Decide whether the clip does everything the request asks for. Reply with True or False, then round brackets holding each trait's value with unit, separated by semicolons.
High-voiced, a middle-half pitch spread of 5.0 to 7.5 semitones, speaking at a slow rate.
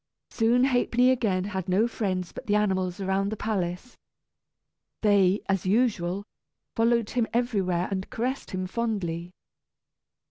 False (200 Hz; 3.9 semitones; 130 wpm)